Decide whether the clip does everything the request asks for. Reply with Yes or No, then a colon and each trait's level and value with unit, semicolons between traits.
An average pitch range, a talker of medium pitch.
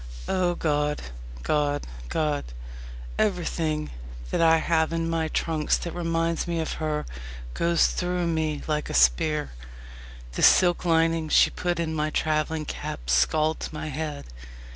No: narrow, 1.6 semitones; medium, 160 Hz